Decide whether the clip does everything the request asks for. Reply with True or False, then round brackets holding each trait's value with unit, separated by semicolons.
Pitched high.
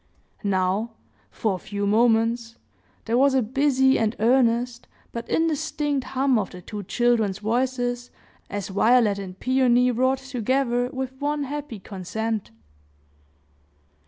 True (240 Hz)